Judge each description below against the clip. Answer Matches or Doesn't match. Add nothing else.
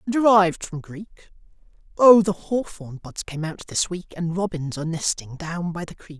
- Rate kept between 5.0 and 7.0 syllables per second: Doesn't match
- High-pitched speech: Doesn't match